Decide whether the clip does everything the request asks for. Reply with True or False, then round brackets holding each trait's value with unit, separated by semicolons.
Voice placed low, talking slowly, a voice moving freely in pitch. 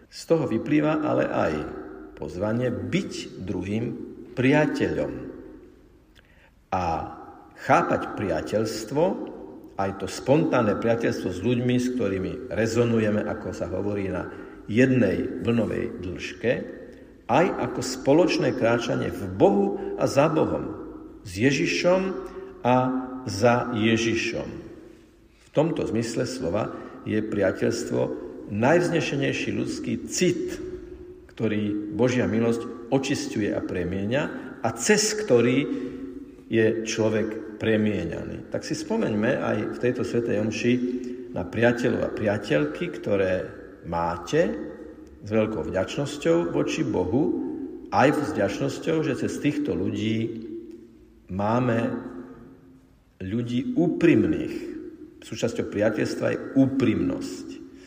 True (120 Hz; 100 wpm; 6.3 semitones)